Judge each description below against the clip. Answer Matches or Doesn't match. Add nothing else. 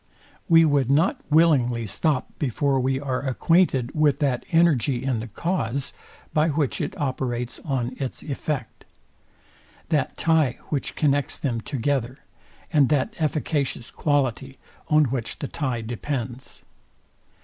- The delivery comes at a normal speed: Doesn't match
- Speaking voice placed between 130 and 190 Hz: Matches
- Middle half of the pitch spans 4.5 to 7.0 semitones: Doesn't match